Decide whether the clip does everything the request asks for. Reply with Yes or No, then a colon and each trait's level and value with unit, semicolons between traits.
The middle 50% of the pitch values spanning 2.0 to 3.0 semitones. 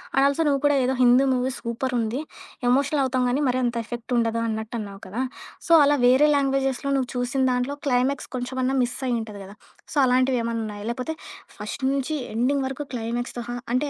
Yes: narrow, 2.4 semitones